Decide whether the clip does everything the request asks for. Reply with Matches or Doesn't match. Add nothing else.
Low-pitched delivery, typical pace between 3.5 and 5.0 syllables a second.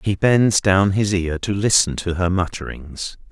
Matches